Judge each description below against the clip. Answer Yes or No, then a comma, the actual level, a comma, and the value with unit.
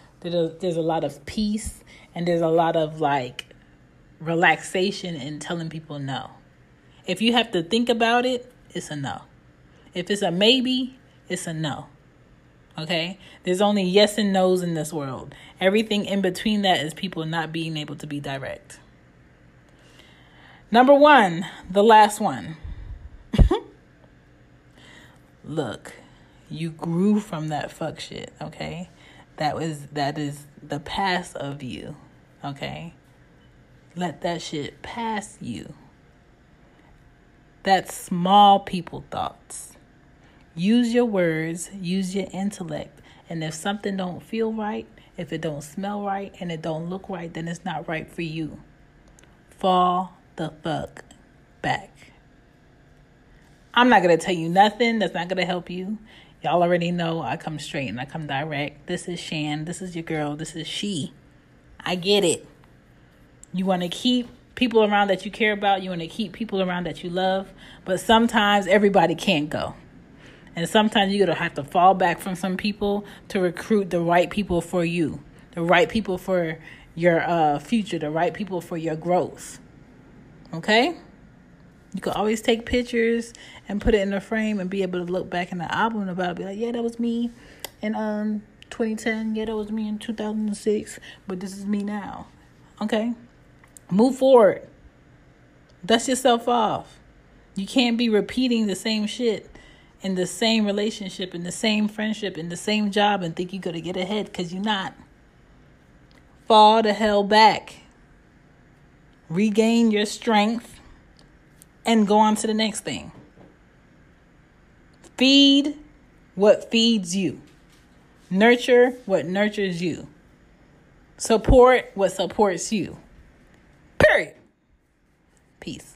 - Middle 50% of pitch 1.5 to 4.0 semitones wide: No, average, 4.5 semitones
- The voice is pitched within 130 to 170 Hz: No, medium, 185 Hz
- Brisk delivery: No, average, 150 wpm